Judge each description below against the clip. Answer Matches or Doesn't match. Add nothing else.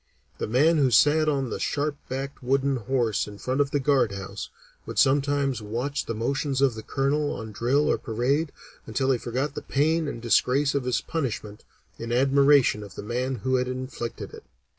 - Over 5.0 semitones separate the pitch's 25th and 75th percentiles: Doesn't match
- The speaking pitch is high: Doesn't match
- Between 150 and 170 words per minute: Doesn't match